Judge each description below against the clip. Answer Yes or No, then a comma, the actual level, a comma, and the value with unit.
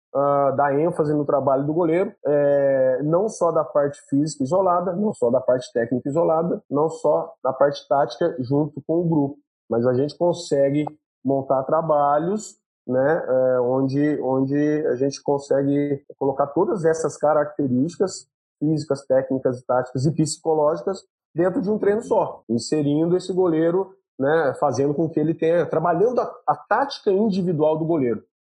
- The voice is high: No, medium, 150 Hz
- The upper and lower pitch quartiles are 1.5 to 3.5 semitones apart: Yes, average, 3.2 semitones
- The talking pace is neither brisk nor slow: Yes, average, 150 wpm